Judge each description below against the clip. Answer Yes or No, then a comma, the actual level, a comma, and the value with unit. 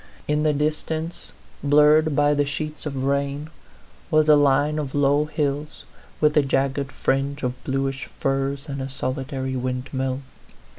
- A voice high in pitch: No, medium, 140 Hz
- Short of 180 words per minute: Yes, average, 145 wpm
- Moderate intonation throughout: No, narrow, 1.9 semitones